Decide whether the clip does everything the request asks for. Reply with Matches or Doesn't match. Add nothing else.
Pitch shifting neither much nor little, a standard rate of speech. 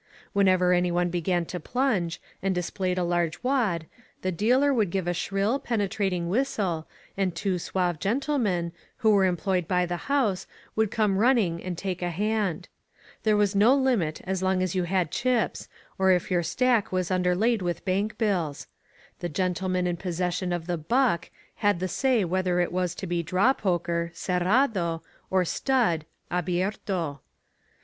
Matches